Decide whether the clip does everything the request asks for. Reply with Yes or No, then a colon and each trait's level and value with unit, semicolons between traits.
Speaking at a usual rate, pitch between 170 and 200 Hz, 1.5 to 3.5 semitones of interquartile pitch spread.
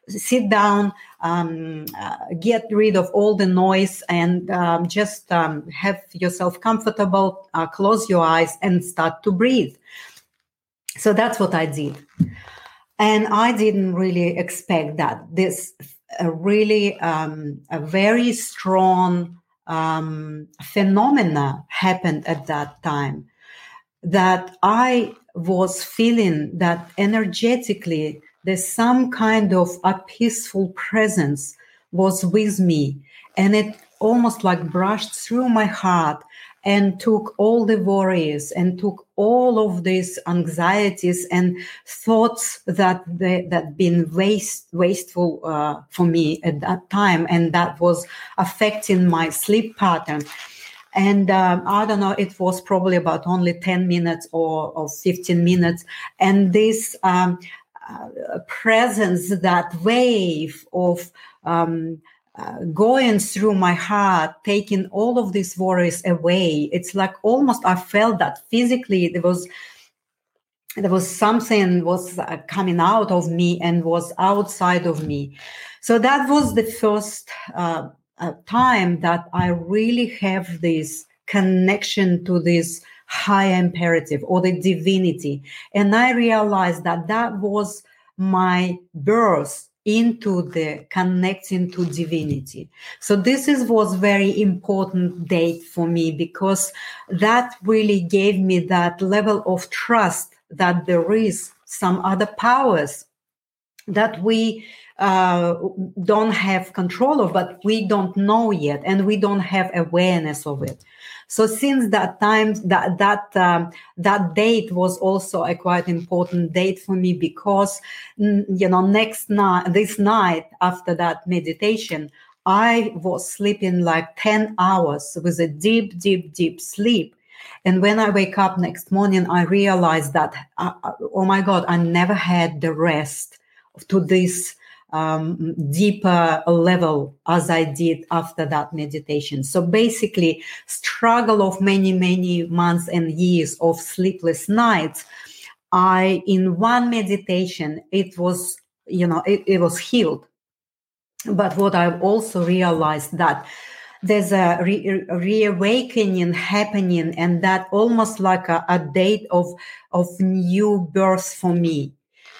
No: slow, 130 wpm; medium, 185 Hz; average, 3.2 semitones